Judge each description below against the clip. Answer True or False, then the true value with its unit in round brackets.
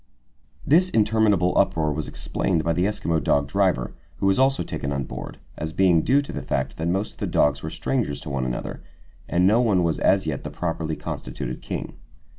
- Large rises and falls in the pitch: True (5.7 semitones)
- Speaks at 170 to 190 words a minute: False (205 wpm)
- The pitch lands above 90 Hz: False (85 Hz)